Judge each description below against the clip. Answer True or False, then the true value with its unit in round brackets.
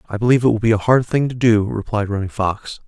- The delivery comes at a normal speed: False (270 wpm)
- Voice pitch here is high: False (110 Hz)